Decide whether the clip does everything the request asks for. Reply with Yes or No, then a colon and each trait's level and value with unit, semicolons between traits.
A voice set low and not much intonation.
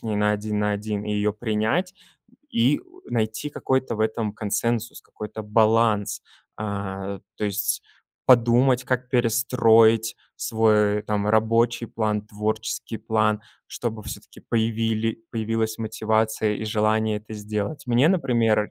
Yes: low, 110 Hz; narrow, 1.6 semitones